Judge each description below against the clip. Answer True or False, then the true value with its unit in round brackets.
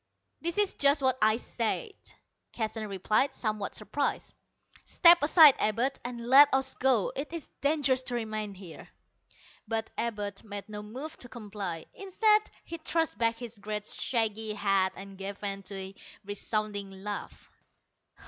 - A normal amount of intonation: True (4.8 semitones)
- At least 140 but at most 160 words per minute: True (150 wpm)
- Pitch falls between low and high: False (220 Hz)